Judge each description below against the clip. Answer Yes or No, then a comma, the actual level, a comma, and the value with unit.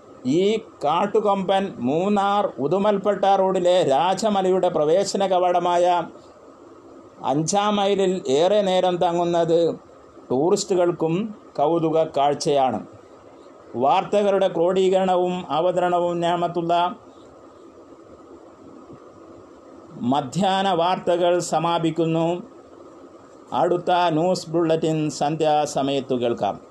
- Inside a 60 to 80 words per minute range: Yes, average, 65 wpm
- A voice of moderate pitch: Yes, medium, 180 Hz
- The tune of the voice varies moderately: Yes, average, 3.0 semitones